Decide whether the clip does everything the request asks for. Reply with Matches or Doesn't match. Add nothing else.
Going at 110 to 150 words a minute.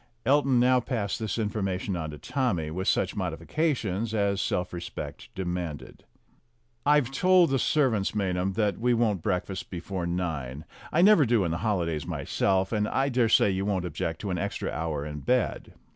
Doesn't match